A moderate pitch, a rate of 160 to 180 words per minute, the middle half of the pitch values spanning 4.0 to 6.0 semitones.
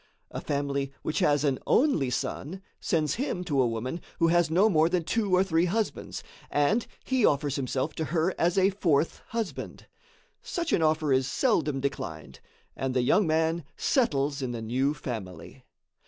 Yes: medium, 155 Hz; average, 170 wpm; average, 5.1 semitones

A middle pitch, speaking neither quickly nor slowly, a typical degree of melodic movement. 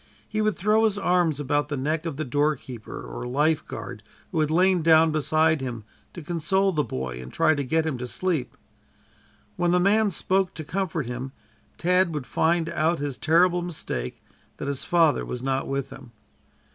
Yes: medium, 155 Hz; average, 185 wpm; average, 4.5 semitones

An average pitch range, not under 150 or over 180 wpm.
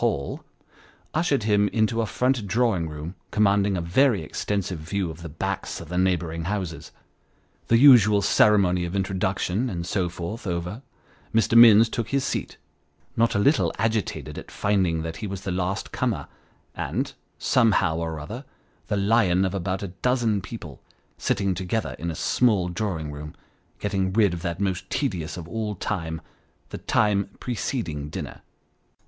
Yes: average, 4.1 semitones; average, 160 wpm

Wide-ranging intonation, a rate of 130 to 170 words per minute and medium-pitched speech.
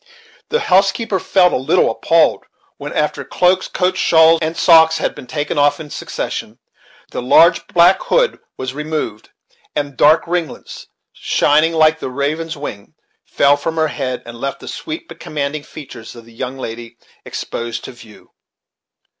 No: average, 4.1 semitones; average, 165 wpm; medium, 155 Hz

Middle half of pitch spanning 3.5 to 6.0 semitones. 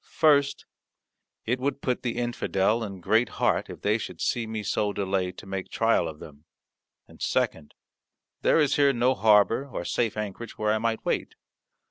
Yes: average, 3.8 semitones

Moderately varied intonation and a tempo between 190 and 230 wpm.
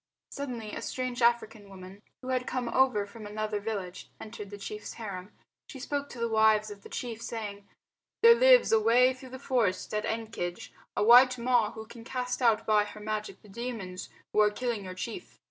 Yes: average, 3.1 semitones; average, 195 wpm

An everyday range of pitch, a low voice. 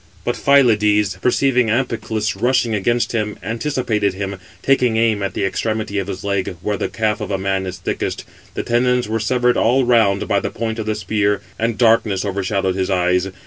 Yes: average, 3.0 semitones; low, 110 Hz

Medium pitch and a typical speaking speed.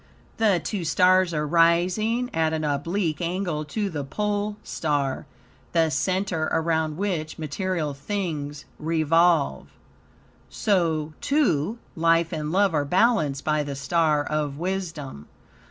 No: medium, 165 Hz; slow, 120 wpm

